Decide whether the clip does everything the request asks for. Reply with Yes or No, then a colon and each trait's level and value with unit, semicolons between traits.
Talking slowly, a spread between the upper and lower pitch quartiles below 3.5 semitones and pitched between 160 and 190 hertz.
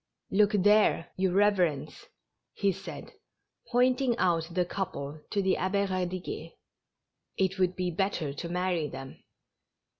Yes: slow, 130 wpm; average, 2.7 semitones; medium, 185 Hz